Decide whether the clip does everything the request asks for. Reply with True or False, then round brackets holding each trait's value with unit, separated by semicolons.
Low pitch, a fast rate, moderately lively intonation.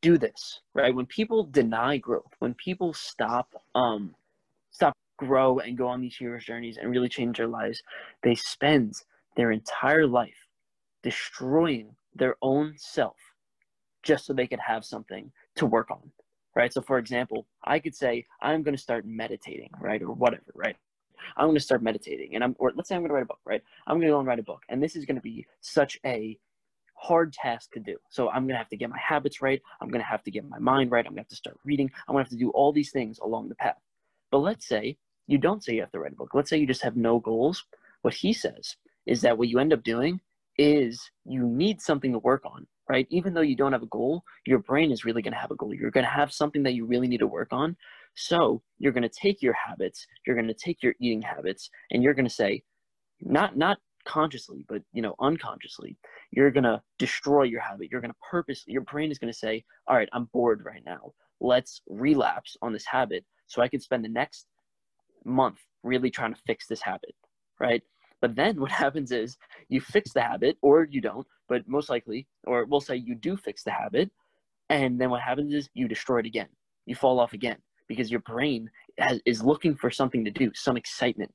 True (130 Hz; 225 wpm; 3.4 semitones)